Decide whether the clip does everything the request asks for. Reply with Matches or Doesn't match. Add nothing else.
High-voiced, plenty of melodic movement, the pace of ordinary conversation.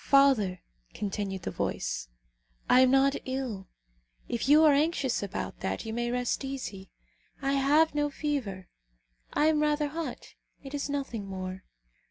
Matches